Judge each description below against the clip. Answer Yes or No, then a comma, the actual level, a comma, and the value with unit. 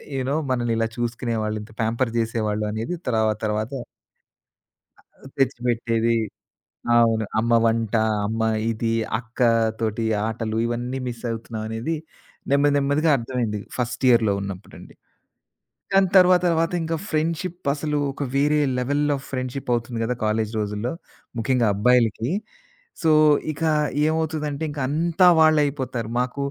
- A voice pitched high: No, low, 120 Hz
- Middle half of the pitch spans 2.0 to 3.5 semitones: No, average, 4.1 semitones